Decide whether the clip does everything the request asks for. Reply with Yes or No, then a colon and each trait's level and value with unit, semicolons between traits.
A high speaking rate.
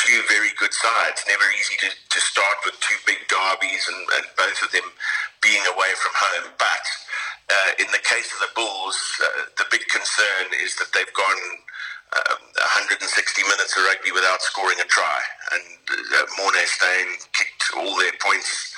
No: average, 175 wpm